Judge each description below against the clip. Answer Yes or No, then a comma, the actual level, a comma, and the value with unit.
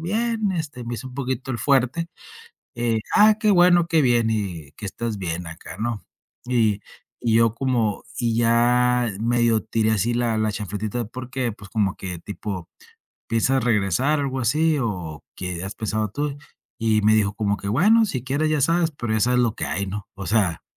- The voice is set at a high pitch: No, low, 115 Hz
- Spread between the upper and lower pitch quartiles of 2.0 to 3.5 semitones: No, average, 4.1 semitones